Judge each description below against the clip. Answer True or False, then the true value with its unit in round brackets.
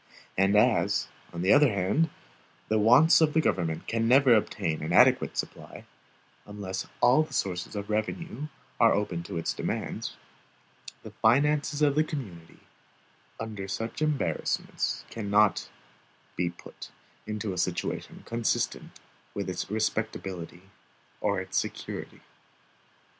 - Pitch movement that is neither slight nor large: False (6.1 semitones)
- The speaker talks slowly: True (125 wpm)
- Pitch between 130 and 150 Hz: False (105 Hz)